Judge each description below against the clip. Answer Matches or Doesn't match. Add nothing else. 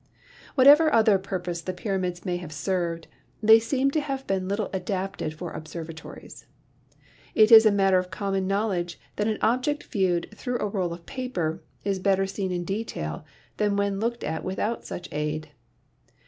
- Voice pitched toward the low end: Doesn't match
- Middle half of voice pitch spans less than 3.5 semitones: Doesn't match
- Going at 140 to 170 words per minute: Matches